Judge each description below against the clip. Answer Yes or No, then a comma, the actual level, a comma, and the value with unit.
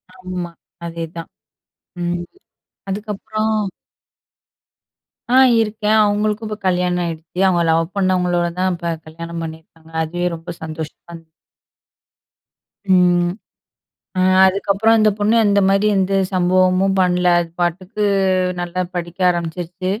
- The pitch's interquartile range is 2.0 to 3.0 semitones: Yes, narrow, 2.5 semitones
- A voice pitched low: No, medium, 180 Hz